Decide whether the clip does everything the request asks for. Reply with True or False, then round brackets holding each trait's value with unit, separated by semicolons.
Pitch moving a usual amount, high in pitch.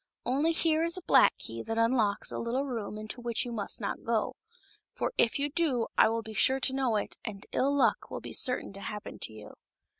True (4.0 semitones; 235 Hz)